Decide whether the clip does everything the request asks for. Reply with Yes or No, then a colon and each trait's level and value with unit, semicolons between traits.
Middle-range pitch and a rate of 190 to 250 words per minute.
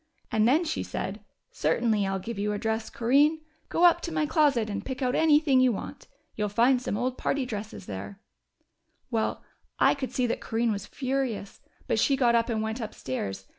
No: high, 235 Hz; average, 195 wpm